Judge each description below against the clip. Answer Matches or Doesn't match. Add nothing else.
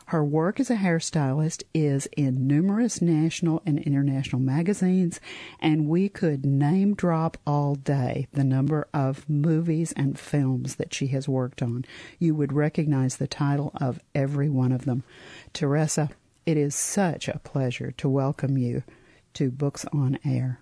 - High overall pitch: Doesn't match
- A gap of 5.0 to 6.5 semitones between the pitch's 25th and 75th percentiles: Doesn't match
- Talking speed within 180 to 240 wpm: Doesn't match